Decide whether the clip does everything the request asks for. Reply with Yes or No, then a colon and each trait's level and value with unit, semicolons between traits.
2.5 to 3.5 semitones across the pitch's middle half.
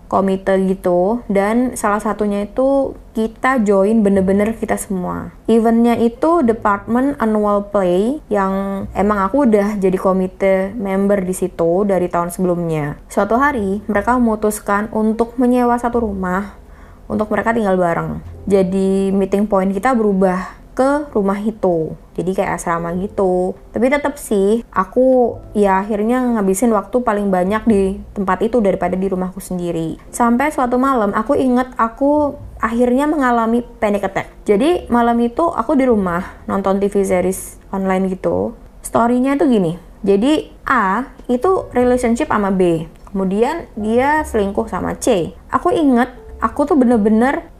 No: average, 3.9 semitones